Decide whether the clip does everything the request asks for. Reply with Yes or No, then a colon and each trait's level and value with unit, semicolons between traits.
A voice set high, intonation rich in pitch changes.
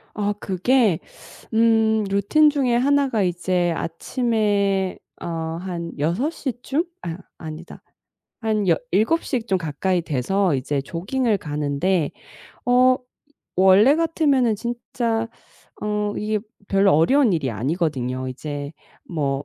Yes: high, 195 Hz; wide, 6.3 semitones